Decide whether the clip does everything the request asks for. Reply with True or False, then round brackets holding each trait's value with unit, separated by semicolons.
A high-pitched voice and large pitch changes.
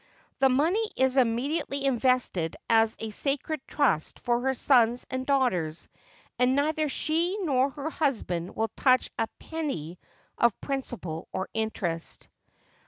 False (255 Hz; 4.2 semitones)